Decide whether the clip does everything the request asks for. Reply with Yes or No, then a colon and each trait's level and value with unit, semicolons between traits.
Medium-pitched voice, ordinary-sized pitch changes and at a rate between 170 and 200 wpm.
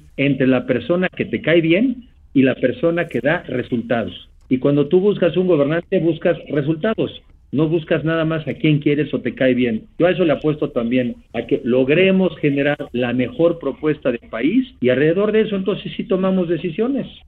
No: medium, 155 Hz; wide, 5.8 semitones; fast, 190 wpm